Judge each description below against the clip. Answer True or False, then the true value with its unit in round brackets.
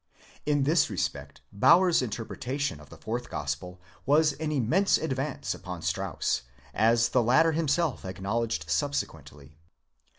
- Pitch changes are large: True (8.6 semitones)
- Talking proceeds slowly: True (130 wpm)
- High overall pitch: False (120 Hz)